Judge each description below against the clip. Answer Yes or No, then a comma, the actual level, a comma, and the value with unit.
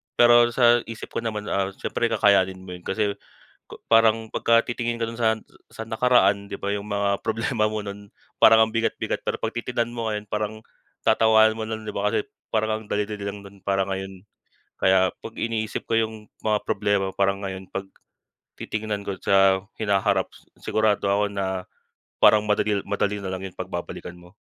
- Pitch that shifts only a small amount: Yes, narrow, 2.2 semitones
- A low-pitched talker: Yes, low, 105 Hz